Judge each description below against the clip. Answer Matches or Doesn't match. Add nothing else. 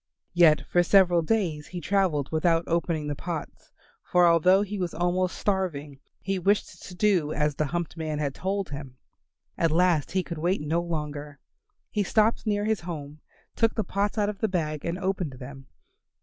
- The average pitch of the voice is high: Doesn't match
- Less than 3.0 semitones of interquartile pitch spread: Doesn't match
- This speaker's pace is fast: Doesn't match